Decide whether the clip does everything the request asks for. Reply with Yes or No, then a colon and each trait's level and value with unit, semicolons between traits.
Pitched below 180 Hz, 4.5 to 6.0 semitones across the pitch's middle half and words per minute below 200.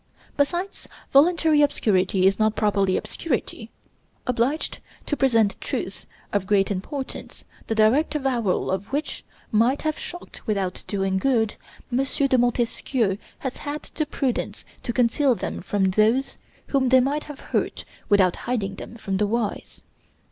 No: high, 235 Hz; average, 5.3 semitones; average, 140 wpm